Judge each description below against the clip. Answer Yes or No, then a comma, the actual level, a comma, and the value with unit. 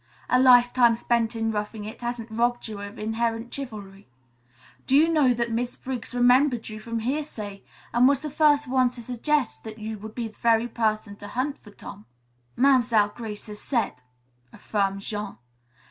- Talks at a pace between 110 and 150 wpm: No, average, 175 wpm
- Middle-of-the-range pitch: No, high, 230 Hz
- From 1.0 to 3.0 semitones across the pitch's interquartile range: Yes, average, 2.7 semitones